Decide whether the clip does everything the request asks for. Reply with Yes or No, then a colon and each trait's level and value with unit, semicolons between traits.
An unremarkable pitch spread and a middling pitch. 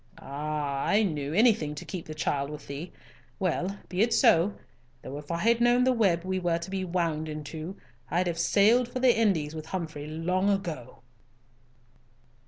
Yes: average, 4.7 semitones; medium, 170 Hz